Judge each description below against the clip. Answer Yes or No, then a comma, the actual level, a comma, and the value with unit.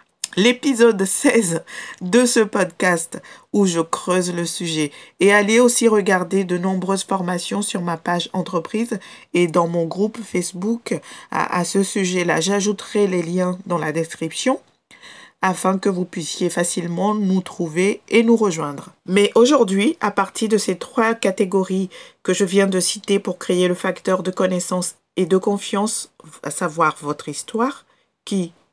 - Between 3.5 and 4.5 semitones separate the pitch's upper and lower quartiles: No, average, 2.8 semitones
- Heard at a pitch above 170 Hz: Yes, high, 190 Hz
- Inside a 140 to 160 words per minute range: Yes, average, 150 wpm